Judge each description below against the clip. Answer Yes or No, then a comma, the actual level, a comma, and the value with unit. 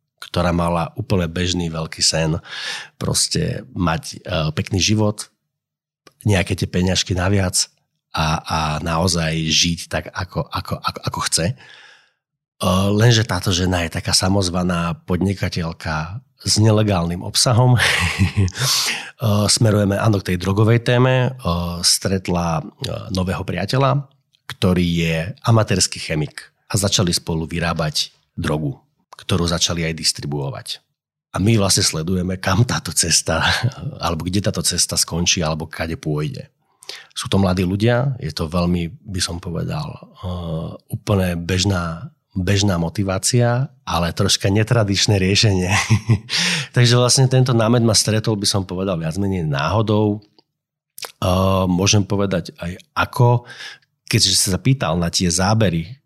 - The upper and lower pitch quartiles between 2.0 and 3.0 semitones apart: No, average, 4.5 semitones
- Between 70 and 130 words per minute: Yes, average, 125 wpm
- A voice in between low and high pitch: No, very low, 95 Hz